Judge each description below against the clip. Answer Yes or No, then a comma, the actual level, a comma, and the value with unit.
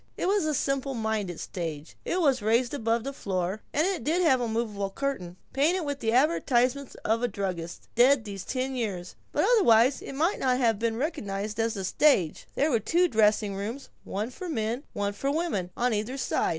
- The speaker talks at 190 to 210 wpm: Yes, average, 200 wpm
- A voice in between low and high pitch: No, high, 235 Hz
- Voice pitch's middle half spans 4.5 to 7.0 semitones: Yes, average, 5.2 semitones